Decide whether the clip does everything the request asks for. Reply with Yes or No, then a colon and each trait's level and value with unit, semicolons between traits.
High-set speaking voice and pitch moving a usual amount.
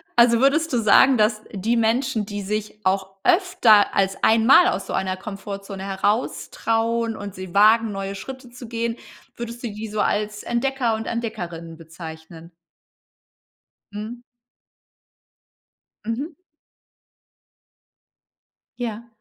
Yes: high, 220 Hz; average, 3.2 semitones